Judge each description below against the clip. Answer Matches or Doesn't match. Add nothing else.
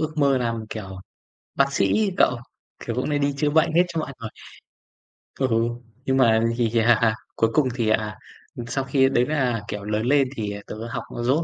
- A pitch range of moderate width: Matches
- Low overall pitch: Matches